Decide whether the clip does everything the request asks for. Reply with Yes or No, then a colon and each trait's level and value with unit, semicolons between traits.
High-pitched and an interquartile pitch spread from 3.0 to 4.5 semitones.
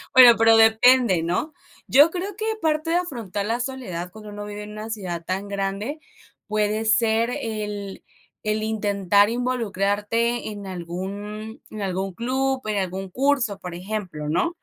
Yes: high, 215 Hz; average, 3.5 semitones